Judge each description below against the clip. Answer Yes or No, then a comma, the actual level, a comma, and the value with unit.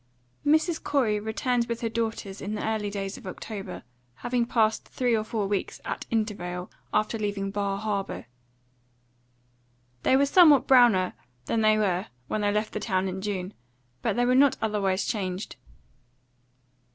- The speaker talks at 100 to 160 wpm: Yes, average, 155 wpm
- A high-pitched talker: Yes, high, 215 Hz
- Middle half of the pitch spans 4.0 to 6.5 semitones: No, average, 3.0 semitones